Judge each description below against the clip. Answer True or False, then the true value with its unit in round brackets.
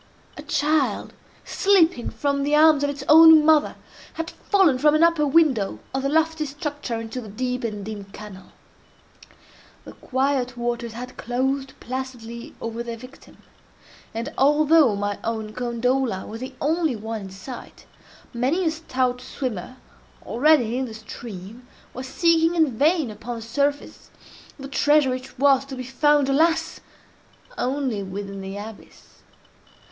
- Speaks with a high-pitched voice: True (260 Hz)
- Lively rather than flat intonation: False (4.5 semitones)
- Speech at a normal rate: True (145 wpm)